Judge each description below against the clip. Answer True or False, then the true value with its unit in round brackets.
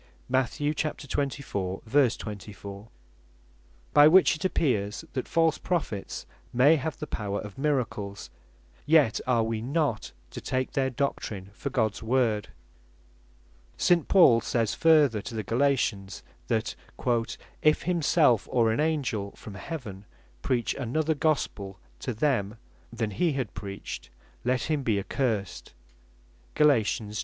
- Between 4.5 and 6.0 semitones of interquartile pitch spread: True (5.6 semitones)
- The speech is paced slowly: True (125 wpm)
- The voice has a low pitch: True (125 Hz)